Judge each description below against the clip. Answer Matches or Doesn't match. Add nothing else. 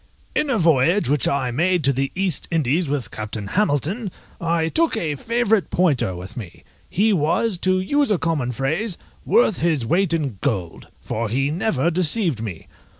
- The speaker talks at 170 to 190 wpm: Matches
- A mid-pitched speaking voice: Matches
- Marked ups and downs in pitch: Matches